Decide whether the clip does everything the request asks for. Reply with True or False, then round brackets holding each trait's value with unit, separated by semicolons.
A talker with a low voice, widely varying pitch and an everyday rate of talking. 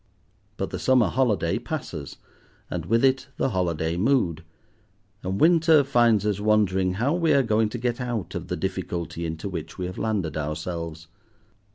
True (105 Hz; 6.4 semitones; 165 wpm)